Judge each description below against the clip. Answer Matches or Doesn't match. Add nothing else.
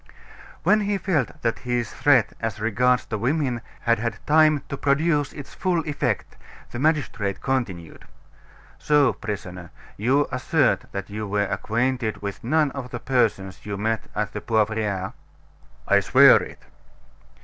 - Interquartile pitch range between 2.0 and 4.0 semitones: Doesn't match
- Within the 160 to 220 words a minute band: Doesn't match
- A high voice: Doesn't match